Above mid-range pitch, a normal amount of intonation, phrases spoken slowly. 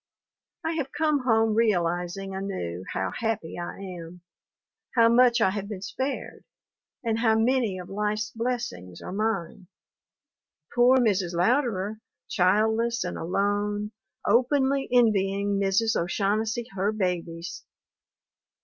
Yes: high, 210 Hz; average, 3.8 semitones; slow, 115 wpm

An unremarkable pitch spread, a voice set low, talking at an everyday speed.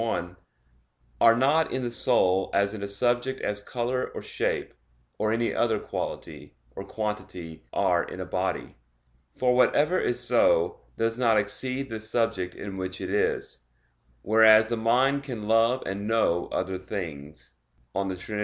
Yes: average, 3.8 semitones; low, 110 Hz; average, 155 wpm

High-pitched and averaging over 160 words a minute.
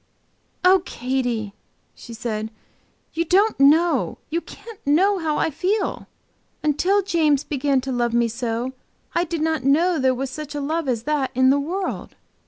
Yes: very high, 290 Hz; average, 170 wpm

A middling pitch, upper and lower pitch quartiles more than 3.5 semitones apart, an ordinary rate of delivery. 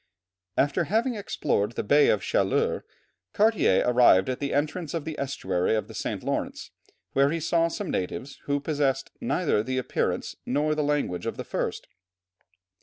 Yes: medium, 145 Hz; average, 4.7 semitones; average, 165 wpm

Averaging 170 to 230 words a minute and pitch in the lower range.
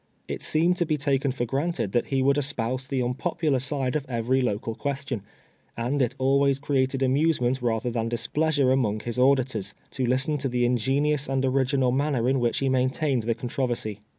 Yes: average, 190 wpm; low, 130 Hz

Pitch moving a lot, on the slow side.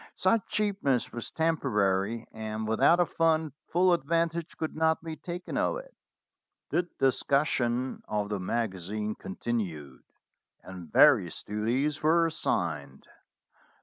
Yes: wide, 7.8 semitones; slow, 120 wpm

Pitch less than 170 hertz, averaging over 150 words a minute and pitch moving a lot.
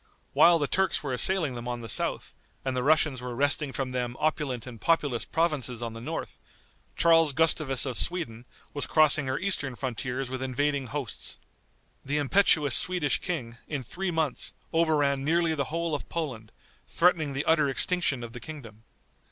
No: medium, 140 Hz; average, 170 wpm; average, 4.2 semitones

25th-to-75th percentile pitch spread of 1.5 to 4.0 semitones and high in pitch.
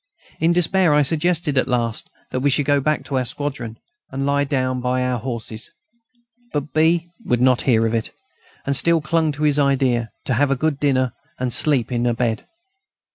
No: average, 3.2 semitones; low, 135 Hz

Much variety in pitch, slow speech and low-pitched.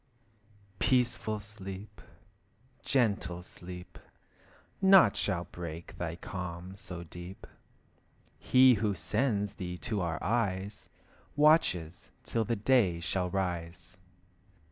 No: average, 3.8 semitones; slow, 100 wpm; very low, 95 Hz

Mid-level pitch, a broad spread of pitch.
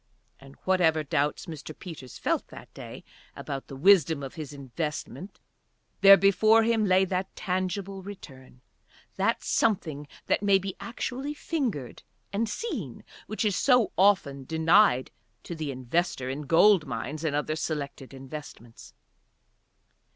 Yes: medium, 165 Hz; wide, 6.0 semitones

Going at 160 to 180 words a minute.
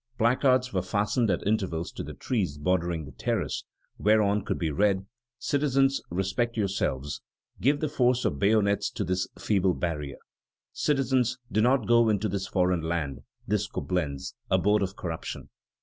No: average, 150 wpm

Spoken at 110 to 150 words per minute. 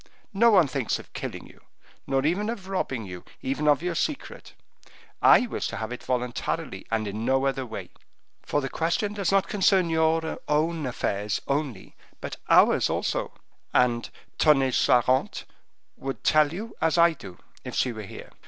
No: average, 170 wpm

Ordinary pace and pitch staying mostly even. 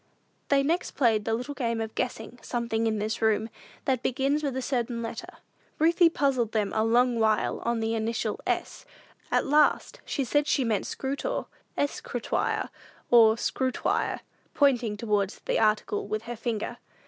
No: average, 160 wpm; average, 3.6 semitones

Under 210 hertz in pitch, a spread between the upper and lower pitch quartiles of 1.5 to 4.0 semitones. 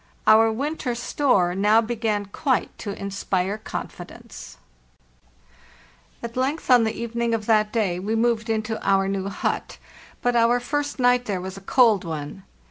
No: high, 220 Hz; average, 3.4 semitones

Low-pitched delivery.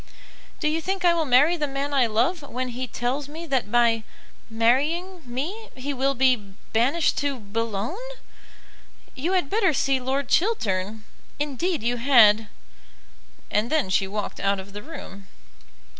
No: very high, 265 Hz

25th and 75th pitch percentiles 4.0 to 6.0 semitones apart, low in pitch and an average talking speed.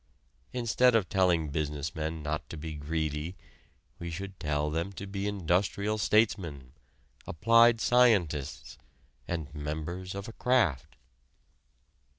No: average, 4.8 semitones; very low, 85 Hz; slow, 120 wpm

